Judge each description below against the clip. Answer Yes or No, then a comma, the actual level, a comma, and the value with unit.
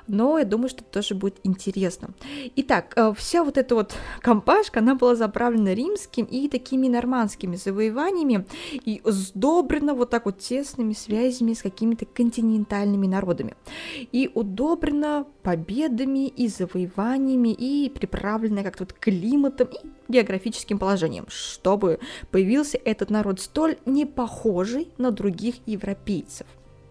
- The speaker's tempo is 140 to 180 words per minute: No, average, 125 wpm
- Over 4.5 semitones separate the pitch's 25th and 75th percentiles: Yes, average, 4.9 semitones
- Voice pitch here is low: No, high, 235 Hz